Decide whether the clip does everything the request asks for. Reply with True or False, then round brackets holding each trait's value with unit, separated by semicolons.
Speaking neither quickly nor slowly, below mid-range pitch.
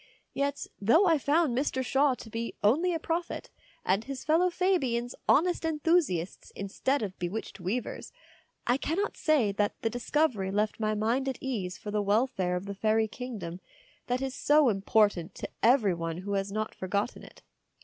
False (170 wpm; 235 Hz)